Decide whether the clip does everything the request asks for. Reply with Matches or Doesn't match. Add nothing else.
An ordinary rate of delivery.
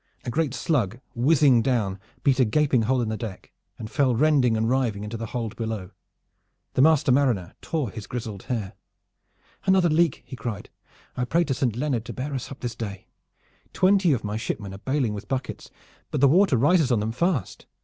Matches